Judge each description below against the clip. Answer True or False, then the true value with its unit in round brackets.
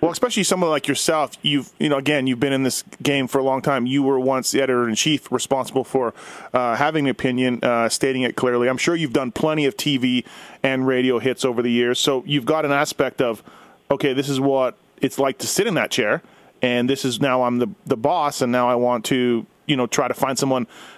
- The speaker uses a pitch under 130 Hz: False (135 Hz)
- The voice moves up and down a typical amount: False (2.2 semitones)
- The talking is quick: True (240 wpm)